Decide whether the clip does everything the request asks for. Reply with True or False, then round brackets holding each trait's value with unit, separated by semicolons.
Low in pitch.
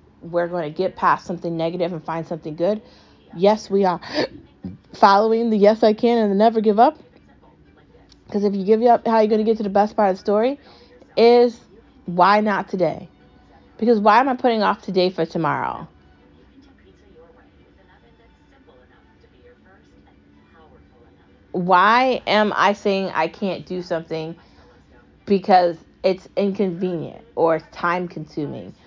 False (185 Hz)